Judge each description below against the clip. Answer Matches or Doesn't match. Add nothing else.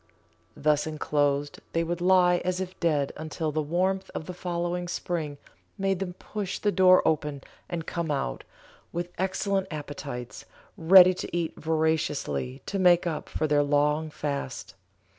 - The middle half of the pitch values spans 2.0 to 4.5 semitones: Matches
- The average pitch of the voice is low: Doesn't match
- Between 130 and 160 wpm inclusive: Matches